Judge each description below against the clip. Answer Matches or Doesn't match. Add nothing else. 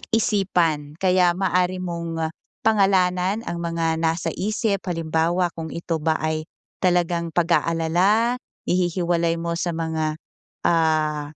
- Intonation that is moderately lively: Doesn't match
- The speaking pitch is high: Doesn't match